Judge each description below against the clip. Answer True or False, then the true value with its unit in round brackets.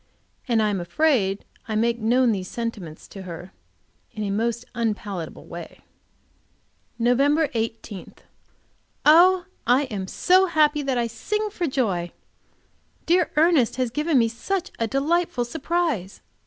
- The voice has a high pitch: True (240 Hz)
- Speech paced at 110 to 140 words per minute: True (135 wpm)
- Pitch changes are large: True (6.4 semitones)